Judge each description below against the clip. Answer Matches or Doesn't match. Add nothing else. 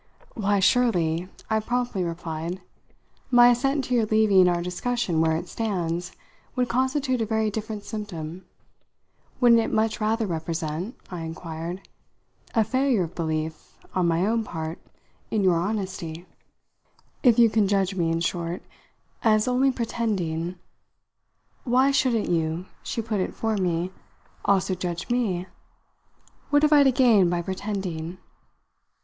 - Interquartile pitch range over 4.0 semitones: Matches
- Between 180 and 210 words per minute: Doesn't match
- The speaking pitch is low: Doesn't match